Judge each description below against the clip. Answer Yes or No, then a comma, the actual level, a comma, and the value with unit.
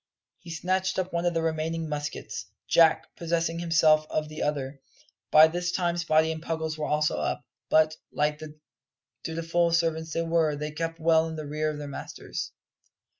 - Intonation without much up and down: Yes, narrow, 1.4 semitones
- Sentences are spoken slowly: No, average, 175 wpm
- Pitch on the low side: No, medium, 160 Hz